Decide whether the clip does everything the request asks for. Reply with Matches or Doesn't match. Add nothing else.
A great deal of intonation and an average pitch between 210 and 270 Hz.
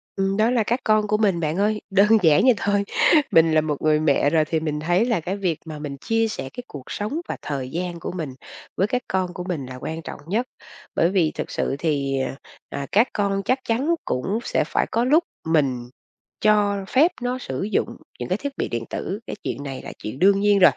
Doesn't match